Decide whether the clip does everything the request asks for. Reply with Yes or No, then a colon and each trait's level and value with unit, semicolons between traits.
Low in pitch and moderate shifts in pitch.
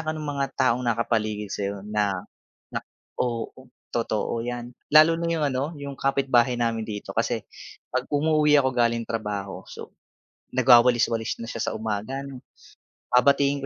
Yes: low, 120 Hz; average, 3.6 semitones